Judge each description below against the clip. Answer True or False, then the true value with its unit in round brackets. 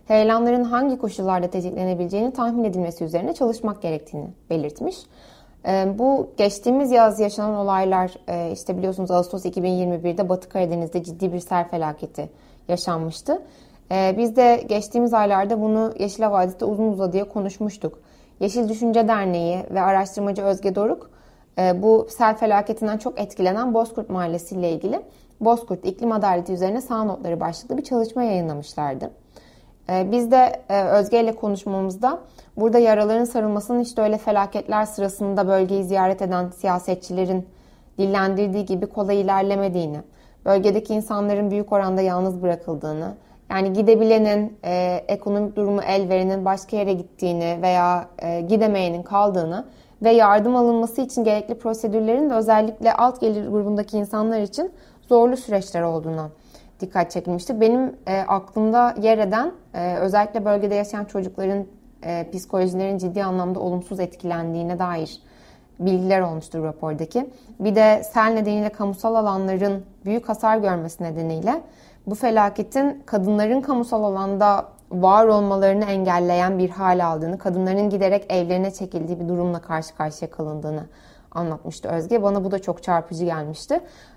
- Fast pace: False (130 wpm)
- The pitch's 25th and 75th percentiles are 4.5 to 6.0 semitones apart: False (3.5 semitones)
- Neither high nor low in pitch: False (200 Hz)